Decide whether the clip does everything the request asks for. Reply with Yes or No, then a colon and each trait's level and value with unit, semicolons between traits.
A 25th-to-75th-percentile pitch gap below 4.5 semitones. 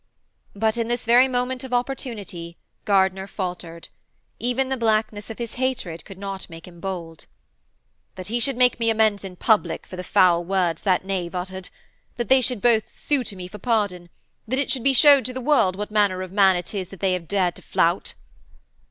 No: average, 4.8 semitones